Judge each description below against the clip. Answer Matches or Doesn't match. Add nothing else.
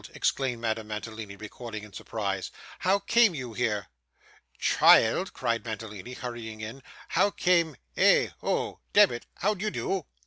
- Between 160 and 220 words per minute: Doesn't match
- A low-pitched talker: Matches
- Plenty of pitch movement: Matches